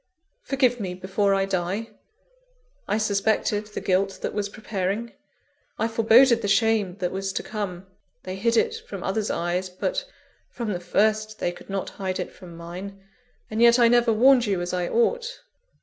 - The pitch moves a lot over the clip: No, average, 3.4 semitones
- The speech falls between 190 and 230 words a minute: No, average, 180 wpm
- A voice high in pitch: Yes, high, 205 Hz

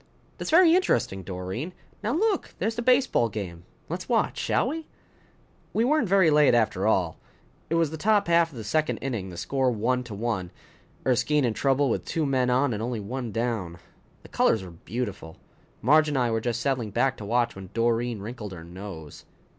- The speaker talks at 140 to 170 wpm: No, average, 195 wpm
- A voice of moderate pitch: No, low, 125 Hz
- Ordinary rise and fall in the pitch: No, wide, 7.1 semitones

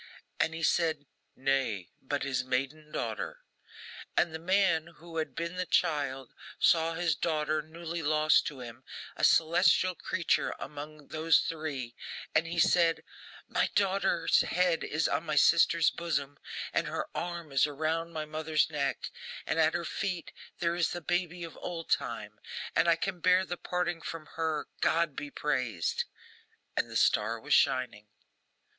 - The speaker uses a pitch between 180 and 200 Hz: No, medium, 160 Hz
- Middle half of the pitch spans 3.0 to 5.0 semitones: No, narrow, 2.5 semitones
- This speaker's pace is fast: No, average, 155 wpm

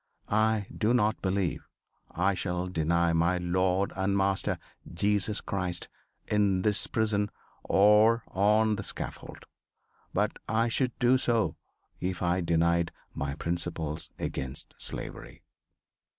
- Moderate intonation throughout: Yes, average, 3.4 semitones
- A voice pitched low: Yes, very low, 95 Hz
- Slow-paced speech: Yes, slow, 120 wpm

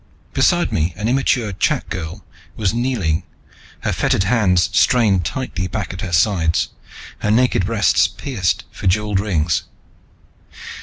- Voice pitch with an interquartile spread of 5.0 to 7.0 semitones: No, average, 4.1 semitones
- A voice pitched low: Yes, very low, 95 Hz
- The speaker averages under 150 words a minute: Yes, slow, 135 wpm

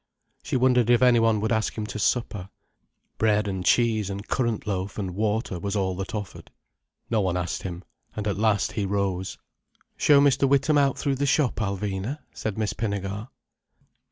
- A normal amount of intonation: Yes, average, 3.4 semitones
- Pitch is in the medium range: No, low, 105 Hz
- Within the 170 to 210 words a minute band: Yes, average, 175 wpm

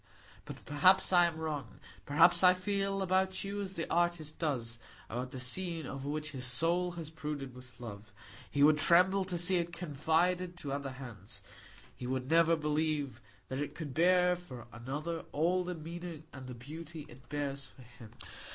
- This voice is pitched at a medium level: Yes, medium, 155 Hz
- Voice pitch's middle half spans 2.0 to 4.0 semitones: No, average, 4.6 semitones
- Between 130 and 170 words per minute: No, average, 180 wpm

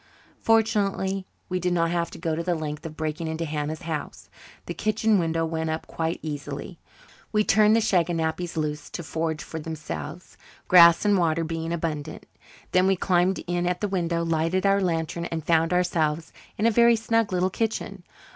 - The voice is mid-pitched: Yes, medium, 170 Hz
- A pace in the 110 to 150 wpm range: No, average, 180 wpm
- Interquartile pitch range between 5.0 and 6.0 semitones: No, average, 2.7 semitones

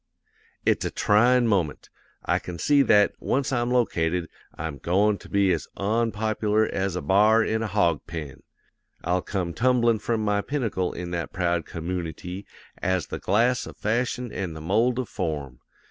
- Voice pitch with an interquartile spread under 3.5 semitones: No, average, 4.8 semitones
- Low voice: Yes, low, 100 Hz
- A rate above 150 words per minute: Yes, average, 165 wpm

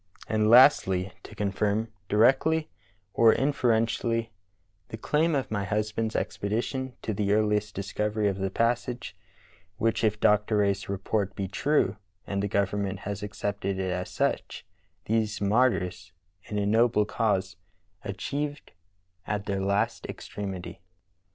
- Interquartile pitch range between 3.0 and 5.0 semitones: No, narrow, 2.4 semitones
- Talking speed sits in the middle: No, slow, 130 wpm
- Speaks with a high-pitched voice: No, low, 105 Hz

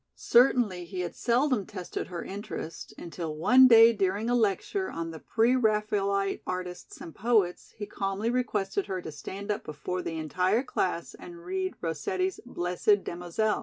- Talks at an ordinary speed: Yes, average, 160 wpm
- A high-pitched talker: Yes, high, 195 Hz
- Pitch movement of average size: Yes, average, 3.8 semitones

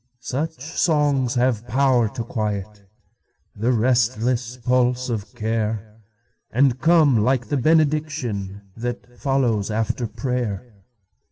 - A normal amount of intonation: Yes, average, 3.4 semitones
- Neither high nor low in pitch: No, low, 120 Hz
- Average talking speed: No, slow, 90 wpm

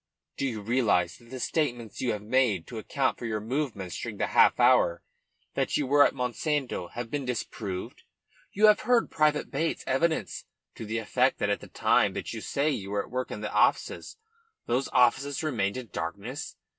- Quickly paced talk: No, average, 195 wpm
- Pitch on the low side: Yes, low, 125 Hz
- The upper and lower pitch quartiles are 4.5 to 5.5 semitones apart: Yes, average, 4.9 semitones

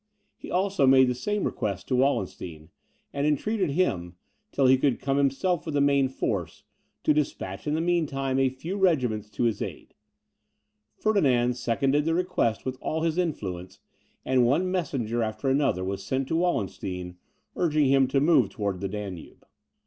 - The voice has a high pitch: No, low, 135 Hz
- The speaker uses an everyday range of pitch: No, wide, 6.3 semitones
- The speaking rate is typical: Yes, average, 170 wpm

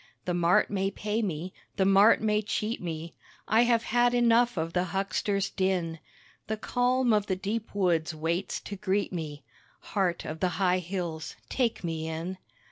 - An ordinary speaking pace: Yes, average, 170 wpm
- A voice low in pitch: No, high, 190 Hz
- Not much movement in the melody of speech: No, average, 4.0 semitones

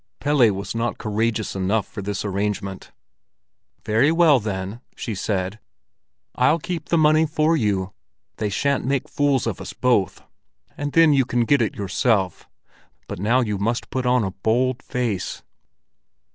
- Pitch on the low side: Yes, low, 115 Hz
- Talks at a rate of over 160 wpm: No, average, 155 wpm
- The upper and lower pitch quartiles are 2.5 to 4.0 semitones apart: No, wide, 5.4 semitones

